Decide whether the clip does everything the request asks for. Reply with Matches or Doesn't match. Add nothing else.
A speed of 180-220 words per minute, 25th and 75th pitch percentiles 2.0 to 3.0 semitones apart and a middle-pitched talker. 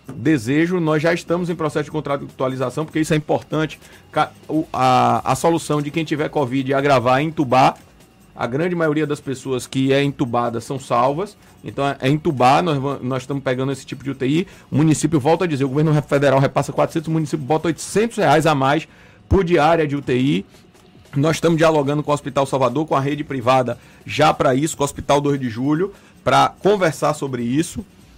Matches